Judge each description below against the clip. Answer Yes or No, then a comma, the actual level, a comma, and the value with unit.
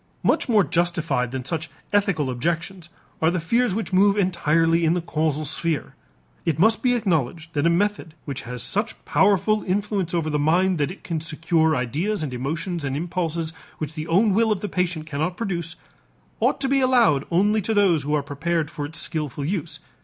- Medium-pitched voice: Yes, medium, 170 Hz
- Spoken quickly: No, average, 190 wpm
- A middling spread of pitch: Yes, average, 4.1 semitones